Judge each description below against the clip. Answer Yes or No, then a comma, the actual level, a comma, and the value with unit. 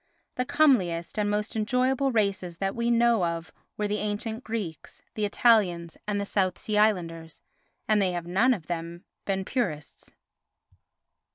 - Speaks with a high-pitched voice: Yes, high, 205 Hz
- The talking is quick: No, average, 155 wpm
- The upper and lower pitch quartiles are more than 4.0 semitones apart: Yes, average, 4.5 semitones